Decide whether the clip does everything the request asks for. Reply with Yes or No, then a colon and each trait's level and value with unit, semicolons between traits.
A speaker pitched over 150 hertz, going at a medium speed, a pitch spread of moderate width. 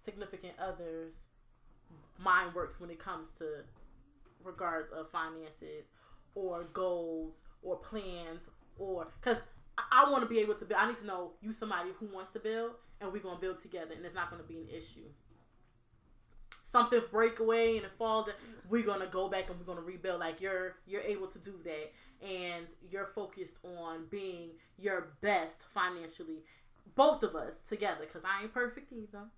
Yes: medium, 185 Hz; average, 170 wpm; average, 4.2 semitones